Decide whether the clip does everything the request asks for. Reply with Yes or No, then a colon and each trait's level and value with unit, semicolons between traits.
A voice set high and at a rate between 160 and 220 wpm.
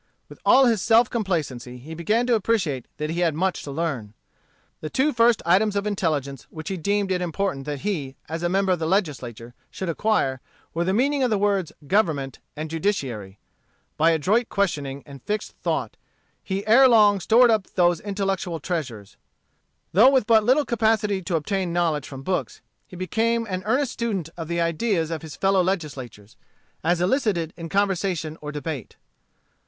No: medium, 180 Hz; average, 175 wpm